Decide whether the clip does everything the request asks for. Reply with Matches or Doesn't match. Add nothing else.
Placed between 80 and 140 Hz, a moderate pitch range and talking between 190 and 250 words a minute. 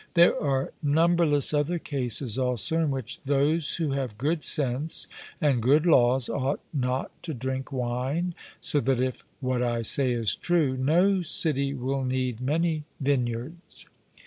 Doesn't match